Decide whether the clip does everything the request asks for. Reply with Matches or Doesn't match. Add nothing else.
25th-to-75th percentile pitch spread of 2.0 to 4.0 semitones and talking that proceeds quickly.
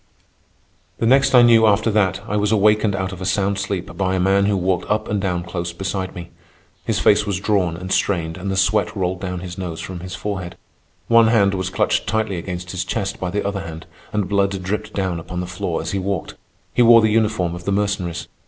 Matches